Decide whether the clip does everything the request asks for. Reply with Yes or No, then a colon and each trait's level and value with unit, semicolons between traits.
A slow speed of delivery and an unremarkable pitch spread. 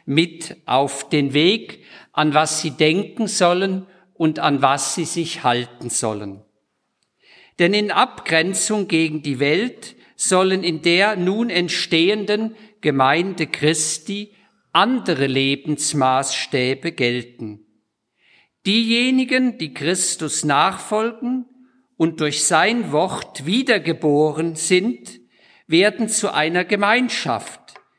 No: slow, 100 wpm; wide, 5.7 semitones